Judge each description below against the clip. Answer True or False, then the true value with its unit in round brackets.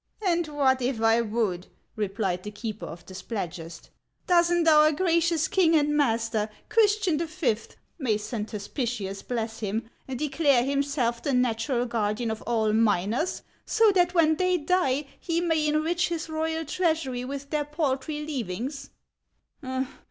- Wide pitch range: True (6.2 semitones)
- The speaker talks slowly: False (160 wpm)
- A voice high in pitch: True (270 Hz)